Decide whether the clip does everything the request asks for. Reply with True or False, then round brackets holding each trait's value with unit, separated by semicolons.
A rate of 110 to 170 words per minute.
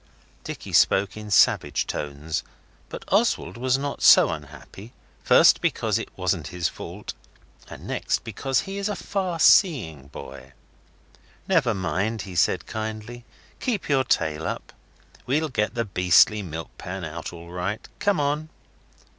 True (145 wpm)